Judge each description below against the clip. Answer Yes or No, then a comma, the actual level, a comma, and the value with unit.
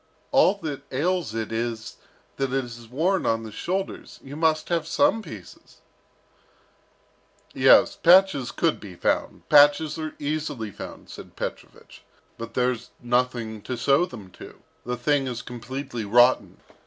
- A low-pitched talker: Yes, low, 130 Hz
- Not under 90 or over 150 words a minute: Yes, average, 145 wpm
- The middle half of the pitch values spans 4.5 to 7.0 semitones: Yes, average, 5.1 semitones